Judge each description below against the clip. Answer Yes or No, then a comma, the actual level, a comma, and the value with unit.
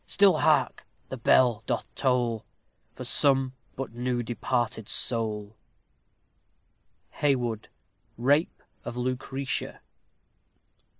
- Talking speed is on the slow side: Yes, slow, 85 wpm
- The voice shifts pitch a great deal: No, narrow, 2.6 semitones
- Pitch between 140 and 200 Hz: No, low, 125 Hz